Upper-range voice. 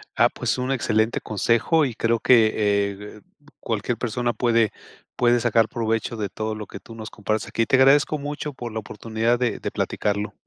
No: low, 115 Hz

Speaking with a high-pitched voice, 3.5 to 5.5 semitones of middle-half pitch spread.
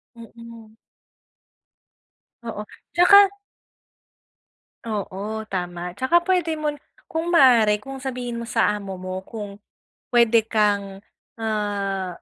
Yes: high, 220 Hz; average, 4.3 semitones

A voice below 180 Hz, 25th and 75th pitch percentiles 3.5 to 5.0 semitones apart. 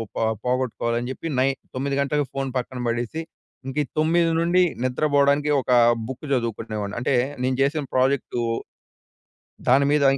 No: low, 135 Hz; average, 2.9 semitones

